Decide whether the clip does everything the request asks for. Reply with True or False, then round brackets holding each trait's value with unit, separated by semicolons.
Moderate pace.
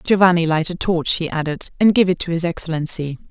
False (220 wpm)